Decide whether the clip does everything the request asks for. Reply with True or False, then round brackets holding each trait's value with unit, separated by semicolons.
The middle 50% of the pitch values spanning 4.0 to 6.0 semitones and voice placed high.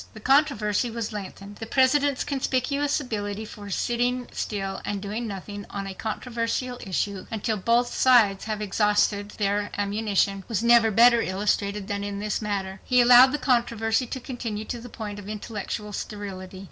False (3.0 semitones; 215 Hz)